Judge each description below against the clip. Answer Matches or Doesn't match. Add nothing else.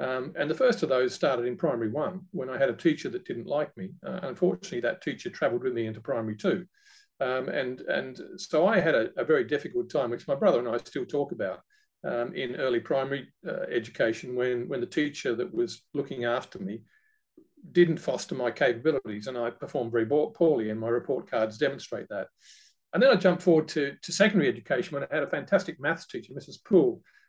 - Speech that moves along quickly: Matches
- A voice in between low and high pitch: Matches